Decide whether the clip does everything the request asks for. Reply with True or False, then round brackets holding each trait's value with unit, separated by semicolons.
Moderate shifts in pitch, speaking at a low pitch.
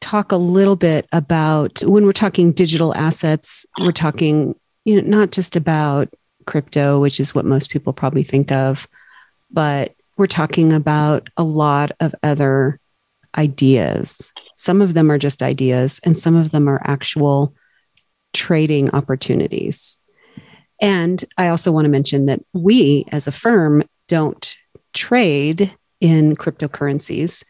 False (3.4 semitones; 155 Hz)